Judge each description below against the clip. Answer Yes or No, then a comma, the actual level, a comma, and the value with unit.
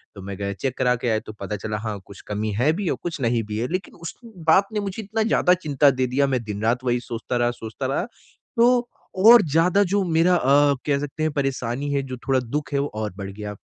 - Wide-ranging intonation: Yes, wide, 6.7 semitones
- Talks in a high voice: No, low, 135 Hz